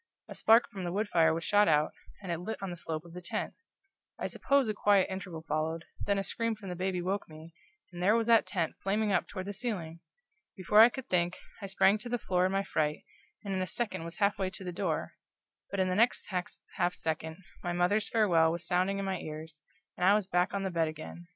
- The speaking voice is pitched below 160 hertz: No, medium, 185 Hz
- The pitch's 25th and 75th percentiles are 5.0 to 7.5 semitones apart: No, average, 3.2 semitones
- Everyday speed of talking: No, fast, 240 wpm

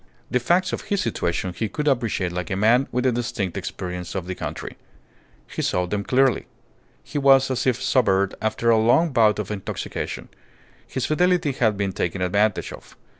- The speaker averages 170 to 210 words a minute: Yes, average, 180 wpm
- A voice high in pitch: No, low, 115 Hz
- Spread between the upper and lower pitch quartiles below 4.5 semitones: No, wide, 5.4 semitones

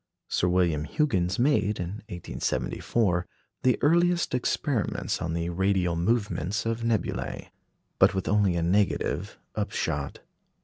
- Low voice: Yes, very low, 95 Hz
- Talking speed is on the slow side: Yes, slow, 120 wpm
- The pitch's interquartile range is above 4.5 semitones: Yes, average, 5.0 semitones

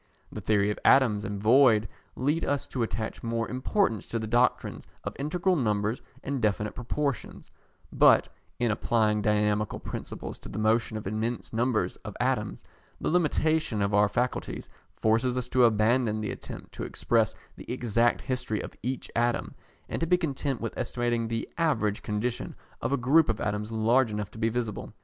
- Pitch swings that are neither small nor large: Yes, average, 3.2 semitones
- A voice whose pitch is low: Yes, low, 115 Hz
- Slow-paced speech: No, average, 175 wpm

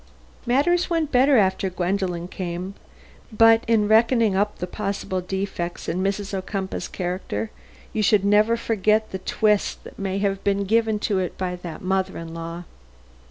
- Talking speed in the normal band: Yes, average, 160 wpm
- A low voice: No, high, 195 Hz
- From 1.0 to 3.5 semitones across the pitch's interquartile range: Yes, average, 2.9 semitones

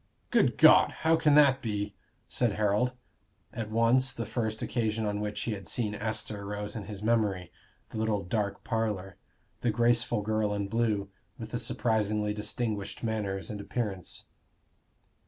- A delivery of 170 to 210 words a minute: No, average, 155 wpm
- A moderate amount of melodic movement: No, narrow, 2.1 semitones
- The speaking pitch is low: Yes, low, 110 Hz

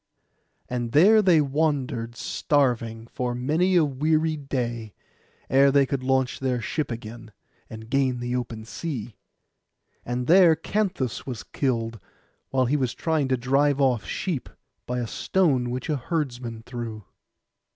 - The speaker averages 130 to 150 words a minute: Yes, average, 140 wpm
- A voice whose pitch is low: Yes, low, 130 Hz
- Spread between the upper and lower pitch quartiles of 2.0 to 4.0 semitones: Yes, average, 3.7 semitones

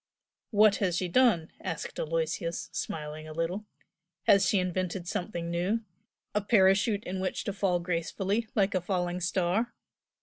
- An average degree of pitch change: Yes, average, 3.0 semitones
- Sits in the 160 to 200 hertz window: Yes, medium, 185 Hz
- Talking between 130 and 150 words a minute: Yes, average, 145 wpm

